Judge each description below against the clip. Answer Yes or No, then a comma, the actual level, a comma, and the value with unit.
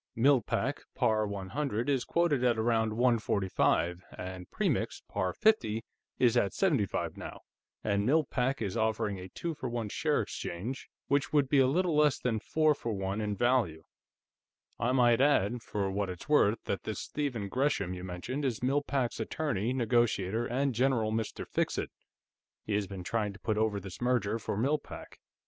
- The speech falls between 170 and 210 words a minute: Yes, average, 175 wpm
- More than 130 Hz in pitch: No, low, 115 Hz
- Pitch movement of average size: Yes, average, 4.7 semitones